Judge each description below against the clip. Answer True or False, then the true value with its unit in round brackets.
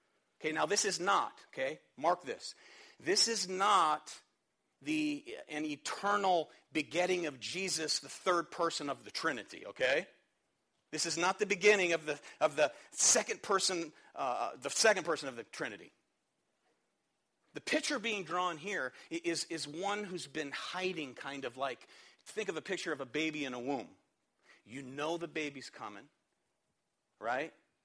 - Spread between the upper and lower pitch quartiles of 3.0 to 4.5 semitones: False (5.0 semitones)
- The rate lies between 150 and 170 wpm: True (155 wpm)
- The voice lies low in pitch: False (175 Hz)